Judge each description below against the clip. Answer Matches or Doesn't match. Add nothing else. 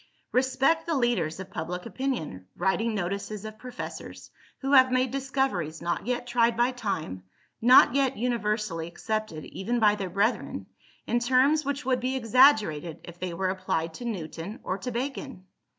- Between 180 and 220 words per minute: Doesn't match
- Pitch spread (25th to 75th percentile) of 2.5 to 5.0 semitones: Doesn't match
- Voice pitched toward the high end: Matches